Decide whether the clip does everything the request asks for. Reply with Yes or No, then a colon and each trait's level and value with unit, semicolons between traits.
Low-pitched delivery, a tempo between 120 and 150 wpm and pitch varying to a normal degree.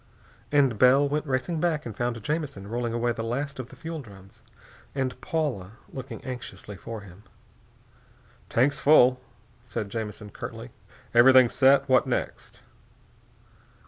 Yes: low, 125 Hz; slow, 135 wpm; average, 3.7 semitones